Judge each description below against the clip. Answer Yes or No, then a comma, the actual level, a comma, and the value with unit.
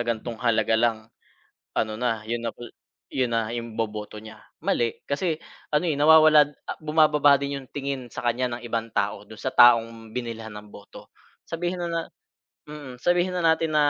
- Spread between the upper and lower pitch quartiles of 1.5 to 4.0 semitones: No, average, 4.9 semitones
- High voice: No, low, 120 Hz